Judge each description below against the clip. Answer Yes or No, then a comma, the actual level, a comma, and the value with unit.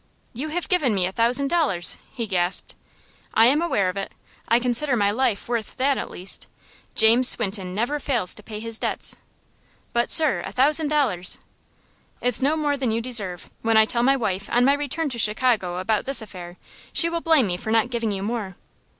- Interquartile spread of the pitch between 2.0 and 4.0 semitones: No, average, 5.1 semitones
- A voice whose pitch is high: Yes, high, 235 Hz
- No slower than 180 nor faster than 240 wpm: Yes, average, 200 wpm